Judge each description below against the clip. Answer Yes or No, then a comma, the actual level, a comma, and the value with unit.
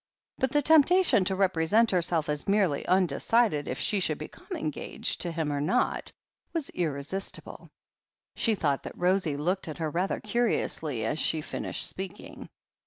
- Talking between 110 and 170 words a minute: Yes, average, 155 wpm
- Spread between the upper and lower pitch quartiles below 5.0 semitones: No, wide, 5.5 semitones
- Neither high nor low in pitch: Yes, medium, 180 Hz